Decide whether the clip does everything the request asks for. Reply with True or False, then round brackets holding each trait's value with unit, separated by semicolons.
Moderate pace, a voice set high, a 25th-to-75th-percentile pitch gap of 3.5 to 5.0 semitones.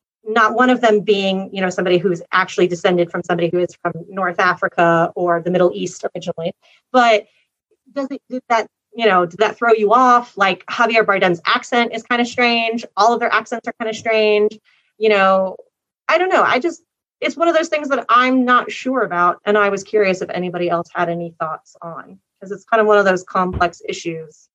False (215 wpm; 205 Hz; 4.7 semitones)